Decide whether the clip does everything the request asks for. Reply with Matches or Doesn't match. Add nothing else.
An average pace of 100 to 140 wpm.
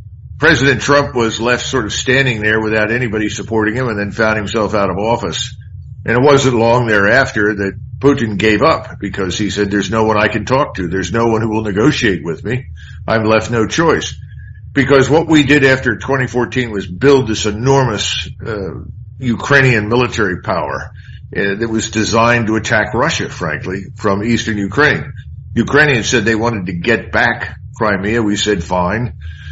Doesn't match